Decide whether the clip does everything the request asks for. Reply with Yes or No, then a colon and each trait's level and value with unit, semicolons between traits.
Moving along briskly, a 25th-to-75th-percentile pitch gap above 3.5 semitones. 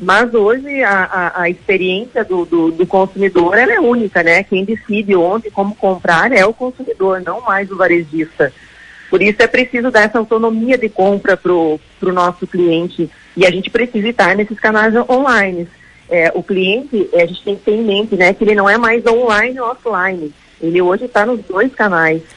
Yes: fast, 195 wpm; average, 4.0 semitones